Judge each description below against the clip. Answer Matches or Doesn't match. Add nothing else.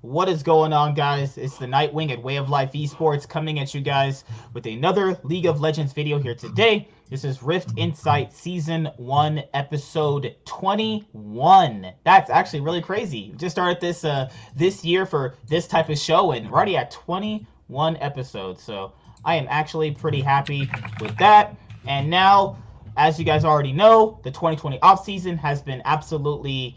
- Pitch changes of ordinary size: Matches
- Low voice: Doesn't match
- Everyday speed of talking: Matches